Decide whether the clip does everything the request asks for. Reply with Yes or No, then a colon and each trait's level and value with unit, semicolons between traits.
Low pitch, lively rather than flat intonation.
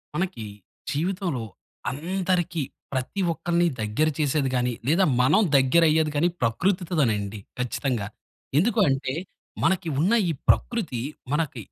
No: medium, 155 Hz; wide, 5.7 semitones